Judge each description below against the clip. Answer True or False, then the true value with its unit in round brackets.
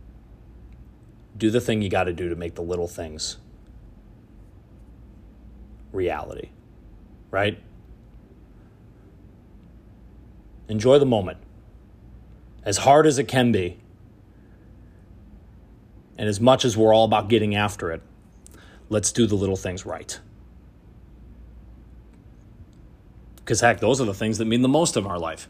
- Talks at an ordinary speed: False (120 wpm)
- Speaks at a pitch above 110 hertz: False (105 Hz)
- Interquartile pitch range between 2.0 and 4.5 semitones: True (2.9 semitones)